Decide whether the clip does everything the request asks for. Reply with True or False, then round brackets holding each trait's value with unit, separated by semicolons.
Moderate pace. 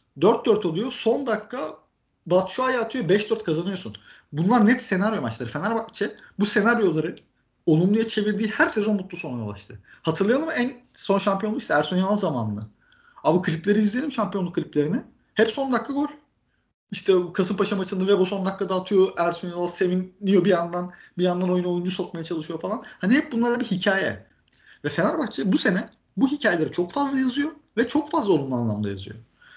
False (165 wpm)